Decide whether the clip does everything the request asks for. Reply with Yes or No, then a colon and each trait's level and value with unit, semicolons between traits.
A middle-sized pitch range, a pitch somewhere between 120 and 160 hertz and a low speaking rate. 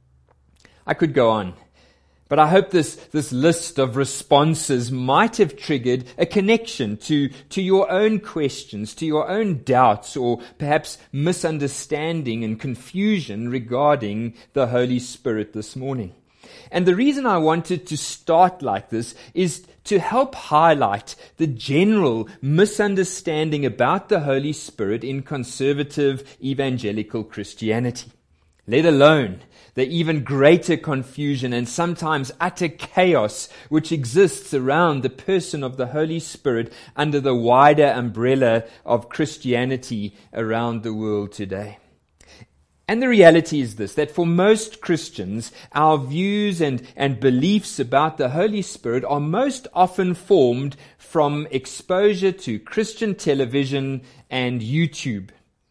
No: wide, 5.7 semitones; medium, 140 Hz; slow, 130 wpm